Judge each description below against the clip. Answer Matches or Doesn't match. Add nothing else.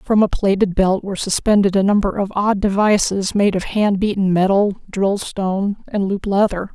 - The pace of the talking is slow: Doesn't match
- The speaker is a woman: Matches